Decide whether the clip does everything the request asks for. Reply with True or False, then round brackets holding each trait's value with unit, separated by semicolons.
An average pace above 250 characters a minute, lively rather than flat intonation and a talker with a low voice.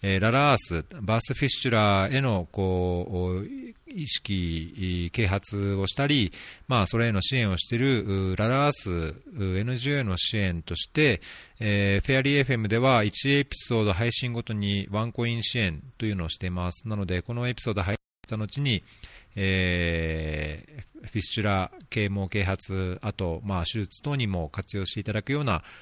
False (325 characters per minute; 4.3 semitones; 105 Hz)